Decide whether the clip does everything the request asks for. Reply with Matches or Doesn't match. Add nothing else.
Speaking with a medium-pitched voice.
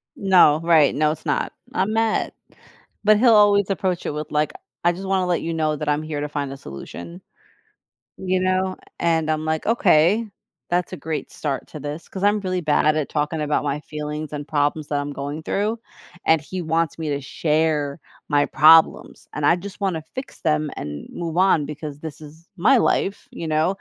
Matches